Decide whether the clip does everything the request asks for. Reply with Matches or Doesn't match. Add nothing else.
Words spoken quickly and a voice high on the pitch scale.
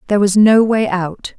Matches